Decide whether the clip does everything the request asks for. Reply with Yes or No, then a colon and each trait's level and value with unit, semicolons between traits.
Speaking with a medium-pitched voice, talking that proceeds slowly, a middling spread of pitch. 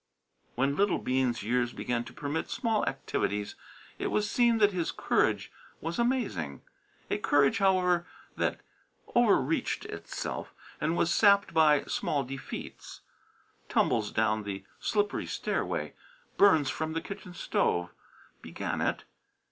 No: medium, 160 Hz; slow, 130 wpm; wide, 7.9 semitones